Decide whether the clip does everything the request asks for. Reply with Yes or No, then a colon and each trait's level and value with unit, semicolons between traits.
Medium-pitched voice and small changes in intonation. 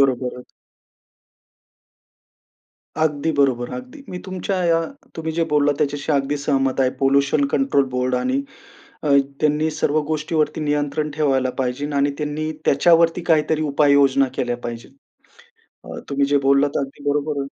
Yes: medium, 145 Hz; narrow, 2.2 semitones